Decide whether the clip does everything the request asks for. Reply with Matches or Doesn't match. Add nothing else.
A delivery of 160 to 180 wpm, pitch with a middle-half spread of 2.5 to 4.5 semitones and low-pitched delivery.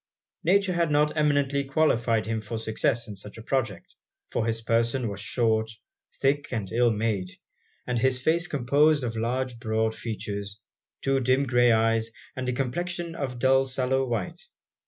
Matches